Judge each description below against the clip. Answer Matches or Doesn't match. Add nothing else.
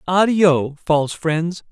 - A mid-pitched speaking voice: Matches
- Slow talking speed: Matches